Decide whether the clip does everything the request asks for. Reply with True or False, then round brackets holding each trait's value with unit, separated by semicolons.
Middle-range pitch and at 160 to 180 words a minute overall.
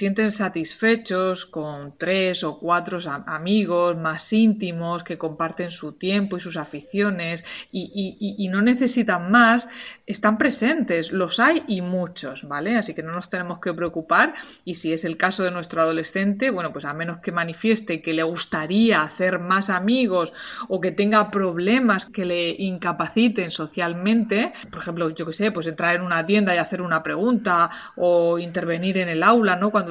True (180 Hz; 170 wpm)